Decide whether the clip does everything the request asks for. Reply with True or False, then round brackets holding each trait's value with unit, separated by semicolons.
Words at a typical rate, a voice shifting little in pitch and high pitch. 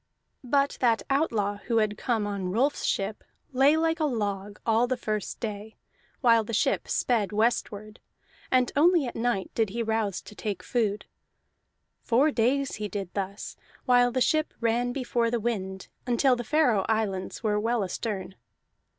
False (160 wpm; 3.2 semitones; 230 Hz)